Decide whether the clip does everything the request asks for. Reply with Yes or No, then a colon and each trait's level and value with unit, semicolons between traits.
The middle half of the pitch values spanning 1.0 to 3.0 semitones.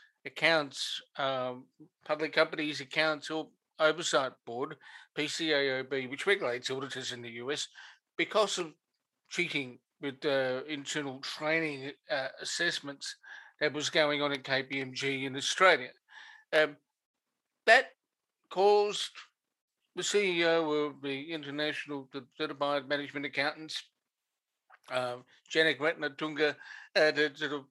Yes: narrow, 2.5 semitones